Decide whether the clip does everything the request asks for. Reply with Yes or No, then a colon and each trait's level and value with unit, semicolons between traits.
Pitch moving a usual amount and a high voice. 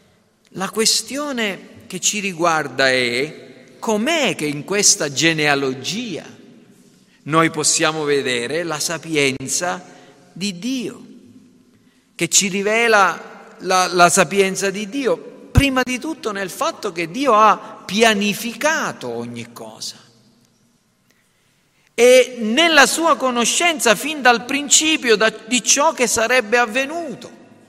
No: wide, 6.9 semitones; high, 215 Hz